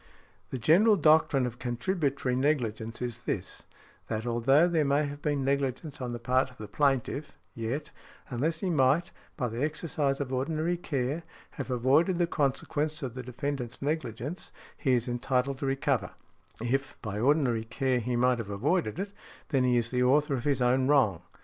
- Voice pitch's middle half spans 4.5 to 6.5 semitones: No, average, 3.3 semitones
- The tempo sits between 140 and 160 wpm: No, average, 175 wpm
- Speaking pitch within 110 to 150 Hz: Yes, low, 135 Hz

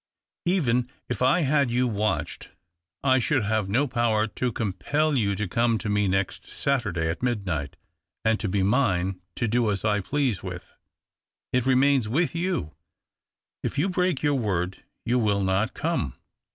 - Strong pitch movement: No, average, 4.9 semitones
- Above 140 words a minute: Yes, average, 165 wpm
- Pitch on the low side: Yes, low, 115 Hz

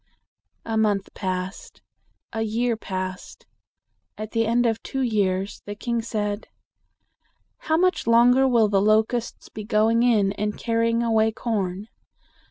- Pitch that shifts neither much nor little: No, narrow, 2.2 semitones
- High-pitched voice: Yes, high, 220 Hz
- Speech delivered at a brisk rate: No, slow, 135 wpm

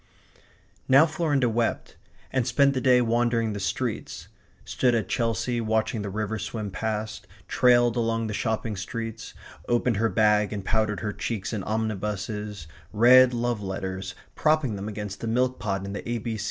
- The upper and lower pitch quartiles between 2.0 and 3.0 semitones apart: Yes, narrow, 2.5 semitones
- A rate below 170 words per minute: Yes, average, 160 wpm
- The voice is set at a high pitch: No, low, 110 Hz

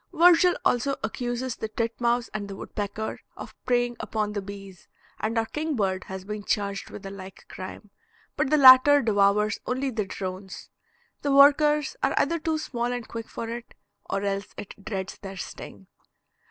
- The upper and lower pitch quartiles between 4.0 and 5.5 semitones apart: Yes, average, 4.5 semitones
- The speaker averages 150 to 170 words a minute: Yes, average, 165 wpm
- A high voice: Yes, high, 220 Hz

